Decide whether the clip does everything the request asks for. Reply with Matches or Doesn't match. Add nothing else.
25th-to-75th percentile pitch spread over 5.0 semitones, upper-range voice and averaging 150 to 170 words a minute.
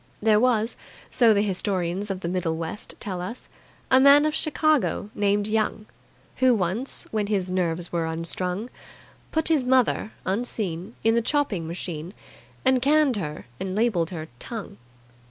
Matches